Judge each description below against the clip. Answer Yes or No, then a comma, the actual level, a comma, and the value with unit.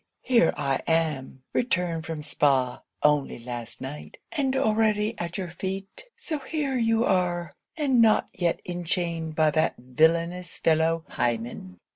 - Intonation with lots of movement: Yes, wide, 6.1 semitones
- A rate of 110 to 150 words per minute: Yes, slow, 135 wpm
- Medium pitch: Yes, medium, 170 Hz